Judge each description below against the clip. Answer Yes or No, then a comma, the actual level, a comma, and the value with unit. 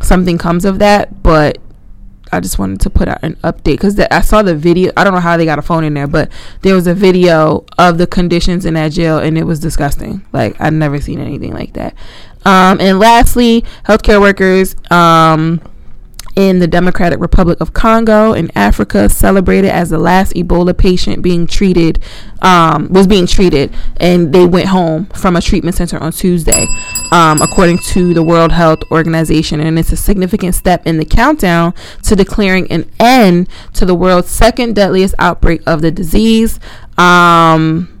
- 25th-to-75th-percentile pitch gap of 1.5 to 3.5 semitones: Yes, average, 2.9 semitones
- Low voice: No, medium, 175 Hz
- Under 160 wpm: No, average, 180 wpm